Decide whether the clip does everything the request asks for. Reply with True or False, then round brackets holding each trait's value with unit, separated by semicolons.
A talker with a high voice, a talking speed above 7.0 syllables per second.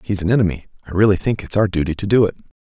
False (100 Hz; 7.6 syllables/s)